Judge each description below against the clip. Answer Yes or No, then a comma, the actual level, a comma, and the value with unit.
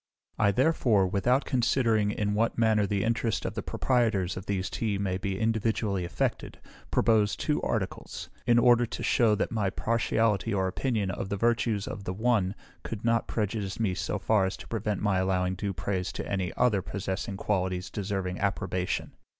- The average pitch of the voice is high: No, low, 105 Hz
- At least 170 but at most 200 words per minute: Yes, average, 175 wpm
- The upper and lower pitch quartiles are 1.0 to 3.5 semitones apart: Yes, average, 3.1 semitones